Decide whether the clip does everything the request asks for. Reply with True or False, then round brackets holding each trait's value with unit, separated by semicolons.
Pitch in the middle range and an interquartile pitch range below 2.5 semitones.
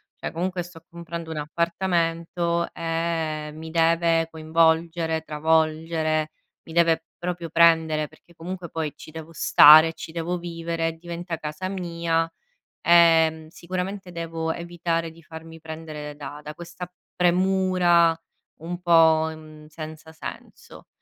True (165 Hz; 1.2 semitones)